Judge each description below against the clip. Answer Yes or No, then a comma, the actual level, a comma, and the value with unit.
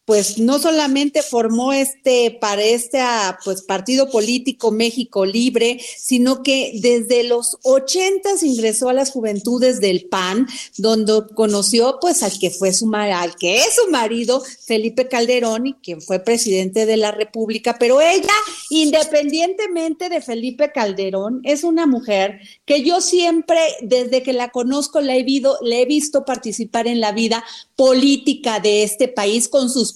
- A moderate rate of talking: Yes, average, 150 wpm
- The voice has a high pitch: Yes, high, 245 Hz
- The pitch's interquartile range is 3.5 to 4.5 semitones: Yes, average, 3.9 semitones